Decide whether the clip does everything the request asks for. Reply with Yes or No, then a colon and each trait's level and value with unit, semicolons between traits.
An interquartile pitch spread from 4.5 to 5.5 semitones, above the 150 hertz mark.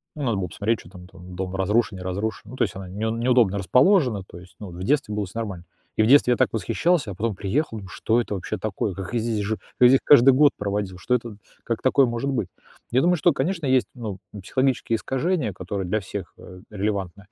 No: average, 4.9 semitones; low, 110 Hz